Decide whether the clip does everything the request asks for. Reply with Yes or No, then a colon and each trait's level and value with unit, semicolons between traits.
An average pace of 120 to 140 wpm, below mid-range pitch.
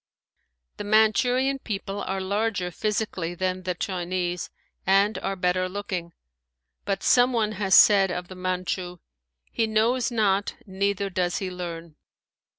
No: slow, 135 wpm; high, 195 Hz